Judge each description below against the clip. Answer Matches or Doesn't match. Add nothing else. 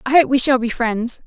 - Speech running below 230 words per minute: Doesn't match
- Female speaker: Matches